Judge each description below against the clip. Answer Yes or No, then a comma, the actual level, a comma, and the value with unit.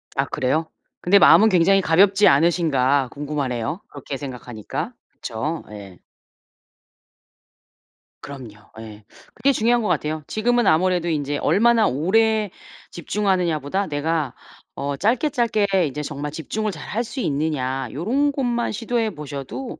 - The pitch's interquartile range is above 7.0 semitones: Yes, wide, 7.4 semitones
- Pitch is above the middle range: No, medium, 160 Hz